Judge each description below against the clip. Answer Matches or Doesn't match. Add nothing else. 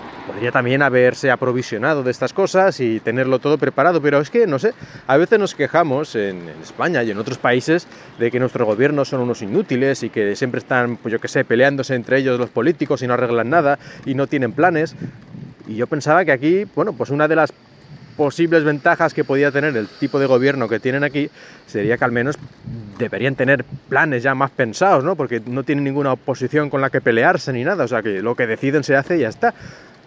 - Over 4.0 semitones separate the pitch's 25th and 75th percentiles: Doesn't match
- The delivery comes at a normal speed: Doesn't match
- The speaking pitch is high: Doesn't match